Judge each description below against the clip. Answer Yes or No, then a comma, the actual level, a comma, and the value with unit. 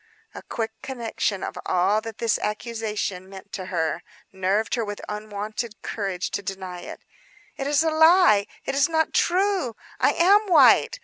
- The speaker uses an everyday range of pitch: No, wide, 6.1 semitones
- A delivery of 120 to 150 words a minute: No, average, 165 wpm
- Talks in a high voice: Yes, high, 215 Hz